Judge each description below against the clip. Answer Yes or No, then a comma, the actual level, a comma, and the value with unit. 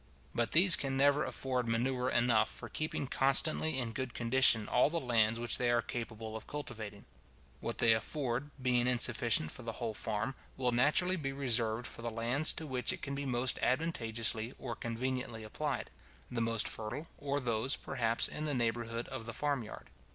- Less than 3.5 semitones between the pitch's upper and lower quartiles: Yes, average, 2.9 semitones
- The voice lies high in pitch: No, low, 120 Hz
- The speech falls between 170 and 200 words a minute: Yes, average, 180 wpm